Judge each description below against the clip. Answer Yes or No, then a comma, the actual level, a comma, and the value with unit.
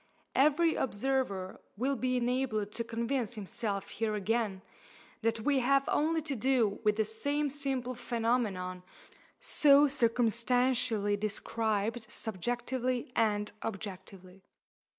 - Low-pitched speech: No, high, 230 Hz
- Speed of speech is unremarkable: No, slow, 110 wpm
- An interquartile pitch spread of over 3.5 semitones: Yes, average, 3.9 semitones